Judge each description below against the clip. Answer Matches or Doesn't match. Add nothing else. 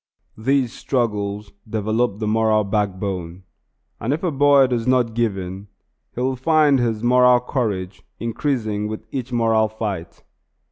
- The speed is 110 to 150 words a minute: Matches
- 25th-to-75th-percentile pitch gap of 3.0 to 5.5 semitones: Matches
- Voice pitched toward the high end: Doesn't match